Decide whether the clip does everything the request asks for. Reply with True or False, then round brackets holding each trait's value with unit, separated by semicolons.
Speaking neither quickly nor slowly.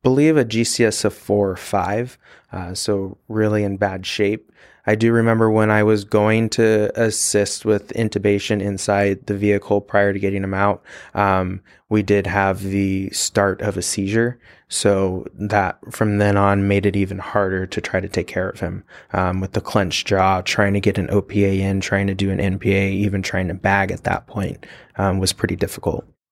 True (190 wpm)